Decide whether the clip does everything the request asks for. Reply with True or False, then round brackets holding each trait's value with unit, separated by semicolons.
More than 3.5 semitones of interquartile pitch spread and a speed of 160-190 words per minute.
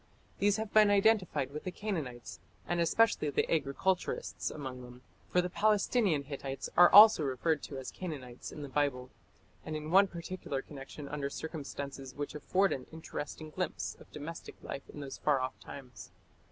True (5.0 semitones; 165 wpm)